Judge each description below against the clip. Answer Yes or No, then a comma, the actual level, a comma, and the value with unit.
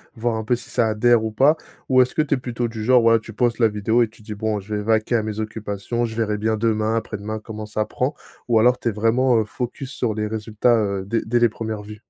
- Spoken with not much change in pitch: Yes, narrow, 2.0 semitones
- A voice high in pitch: No, low, 110 Hz